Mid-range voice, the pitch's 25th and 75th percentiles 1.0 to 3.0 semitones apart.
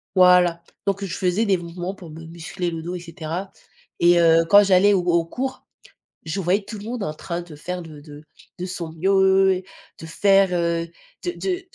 Yes: medium, 180 Hz; average, 2.7 semitones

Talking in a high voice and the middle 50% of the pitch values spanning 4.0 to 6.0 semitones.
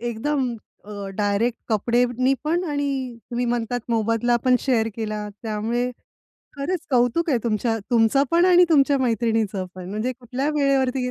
No: high, 245 Hz; average, 3.3 semitones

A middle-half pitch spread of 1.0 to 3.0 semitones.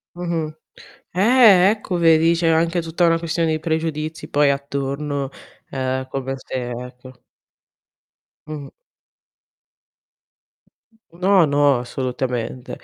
No: average, 3.8 semitones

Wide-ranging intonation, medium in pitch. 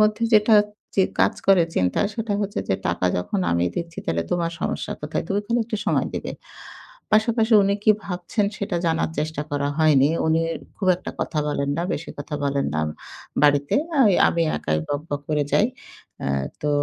Yes: wide, 6.0 semitones; medium, 165 Hz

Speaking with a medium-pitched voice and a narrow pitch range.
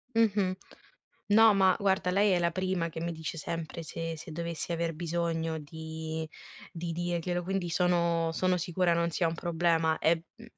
Yes: medium, 170 Hz; narrow, 1.9 semitones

